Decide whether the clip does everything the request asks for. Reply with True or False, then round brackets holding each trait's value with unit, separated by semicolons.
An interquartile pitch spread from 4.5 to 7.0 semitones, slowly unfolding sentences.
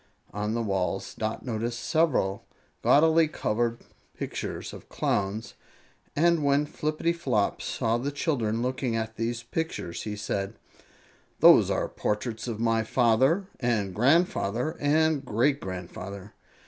True (5.5 semitones; 120 wpm)